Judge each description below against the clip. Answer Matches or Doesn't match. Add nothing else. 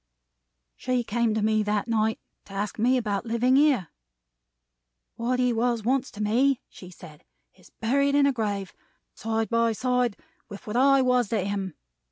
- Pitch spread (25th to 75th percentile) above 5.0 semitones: Doesn't match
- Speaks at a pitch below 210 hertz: Doesn't match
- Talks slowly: Doesn't match